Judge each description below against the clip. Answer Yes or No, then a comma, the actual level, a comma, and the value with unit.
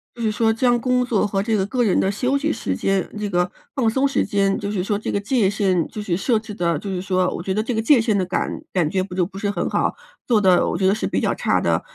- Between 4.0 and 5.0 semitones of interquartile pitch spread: No, average, 3.2 semitones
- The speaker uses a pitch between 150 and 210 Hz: Yes, high, 205 Hz